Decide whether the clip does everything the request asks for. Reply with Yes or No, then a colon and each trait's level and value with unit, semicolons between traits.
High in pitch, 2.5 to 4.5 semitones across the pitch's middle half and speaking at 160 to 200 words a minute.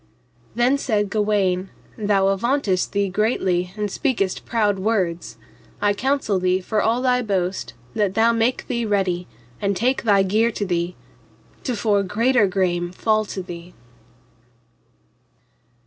No: high, 205 Hz; average, 3.5 semitones; slow, 135 wpm